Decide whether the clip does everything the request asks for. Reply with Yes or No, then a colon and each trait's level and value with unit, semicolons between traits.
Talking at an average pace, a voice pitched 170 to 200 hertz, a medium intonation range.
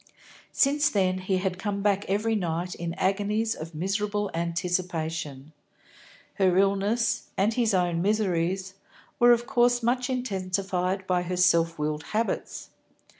No: slow, 130 wpm; high, 190 Hz; average, 3.2 semitones